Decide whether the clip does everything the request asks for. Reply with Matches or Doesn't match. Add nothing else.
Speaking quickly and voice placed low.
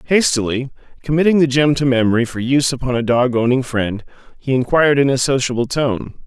Doesn't match